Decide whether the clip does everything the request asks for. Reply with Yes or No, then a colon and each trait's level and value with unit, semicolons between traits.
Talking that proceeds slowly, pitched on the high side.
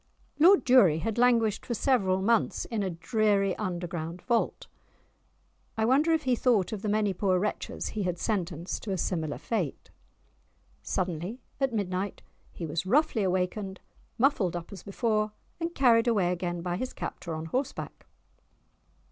No: average, 155 wpm; high, 200 Hz